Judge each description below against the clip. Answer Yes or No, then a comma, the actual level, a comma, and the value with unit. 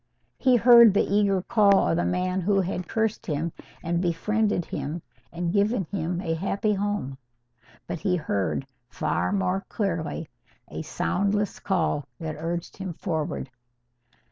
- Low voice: No, medium, 185 Hz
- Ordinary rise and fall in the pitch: Yes, average, 3.8 semitones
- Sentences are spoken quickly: No, average, 140 wpm